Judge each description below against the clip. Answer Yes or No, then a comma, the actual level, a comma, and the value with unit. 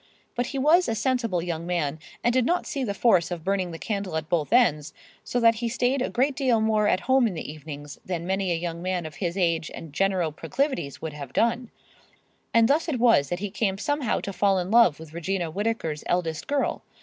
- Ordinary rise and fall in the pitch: No, wide, 6.3 semitones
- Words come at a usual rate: No, fast, 230 wpm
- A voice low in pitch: No, high, 195 Hz